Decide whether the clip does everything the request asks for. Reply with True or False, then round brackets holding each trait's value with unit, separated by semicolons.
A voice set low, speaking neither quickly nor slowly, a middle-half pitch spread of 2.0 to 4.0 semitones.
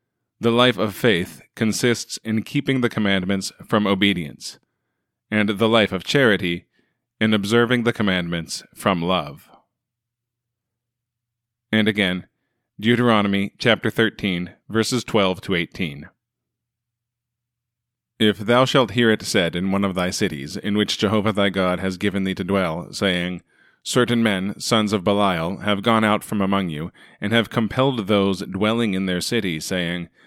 True (105 Hz; 145 wpm; 3.6 semitones)